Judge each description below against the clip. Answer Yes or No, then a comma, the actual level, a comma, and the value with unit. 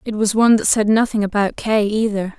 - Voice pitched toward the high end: Yes, high, 210 Hz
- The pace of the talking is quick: Yes, fast, 225 wpm